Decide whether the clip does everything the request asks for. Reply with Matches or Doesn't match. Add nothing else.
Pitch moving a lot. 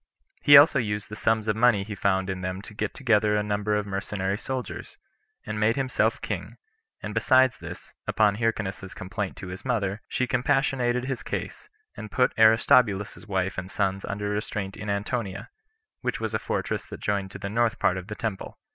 Doesn't match